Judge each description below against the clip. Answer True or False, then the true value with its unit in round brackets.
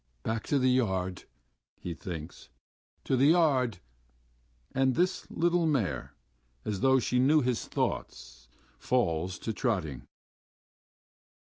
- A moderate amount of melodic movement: False (6.7 semitones)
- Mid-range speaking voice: False (125 Hz)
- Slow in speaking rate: True (115 wpm)